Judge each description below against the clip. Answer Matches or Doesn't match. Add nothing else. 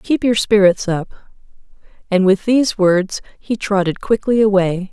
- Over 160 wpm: Doesn't match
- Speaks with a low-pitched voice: Doesn't match